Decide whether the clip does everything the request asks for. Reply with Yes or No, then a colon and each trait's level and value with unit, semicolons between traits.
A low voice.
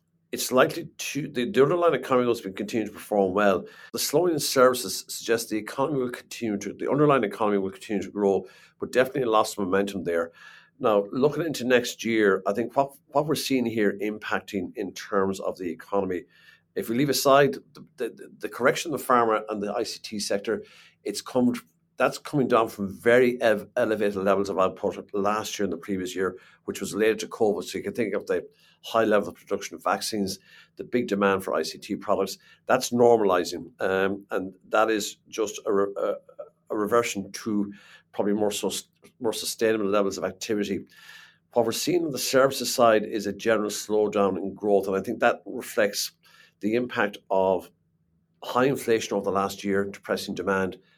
Yes: low, 105 Hz